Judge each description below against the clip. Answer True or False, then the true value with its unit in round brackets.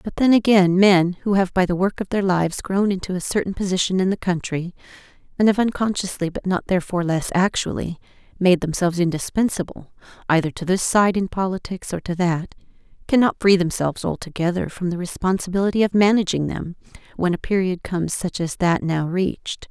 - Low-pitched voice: False (185 Hz)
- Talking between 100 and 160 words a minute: False (180 wpm)